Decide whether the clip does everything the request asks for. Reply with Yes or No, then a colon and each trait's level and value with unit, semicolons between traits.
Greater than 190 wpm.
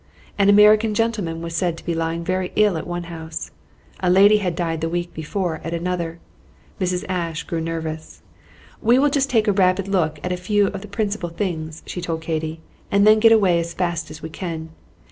Yes: fast, 205 wpm